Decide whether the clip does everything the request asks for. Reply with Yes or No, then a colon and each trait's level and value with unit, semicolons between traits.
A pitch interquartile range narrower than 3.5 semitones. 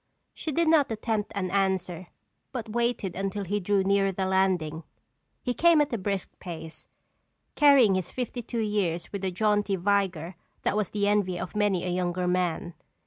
Yes: average, 2.8 semitones